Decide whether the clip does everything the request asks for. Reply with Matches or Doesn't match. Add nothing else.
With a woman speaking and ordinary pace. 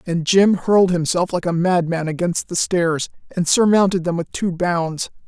Matches